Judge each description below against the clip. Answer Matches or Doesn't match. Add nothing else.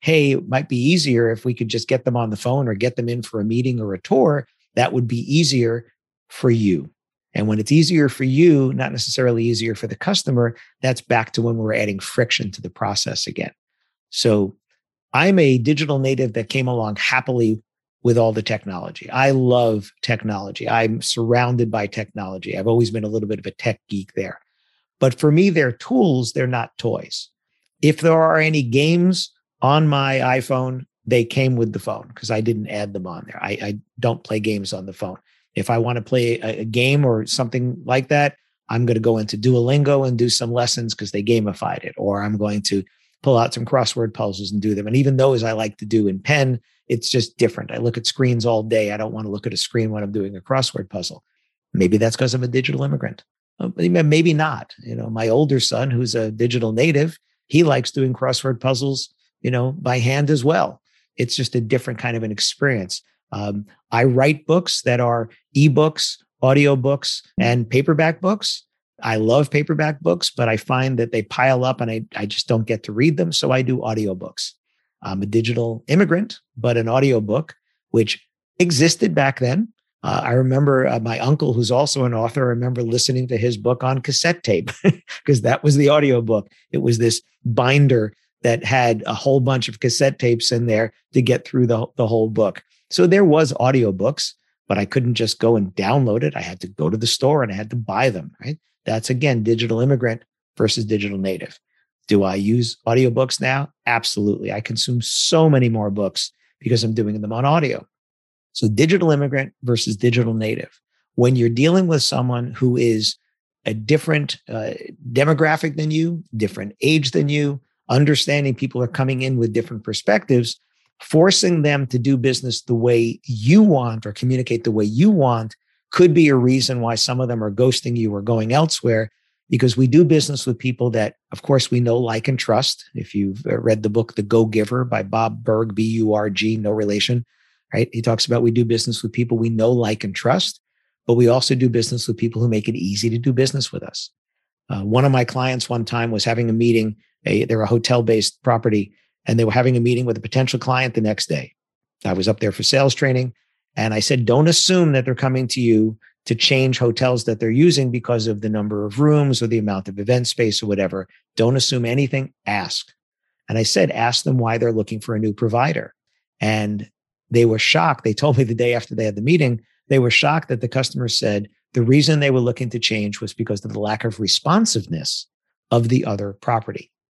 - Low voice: Matches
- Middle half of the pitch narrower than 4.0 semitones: Matches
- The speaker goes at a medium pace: Doesn't match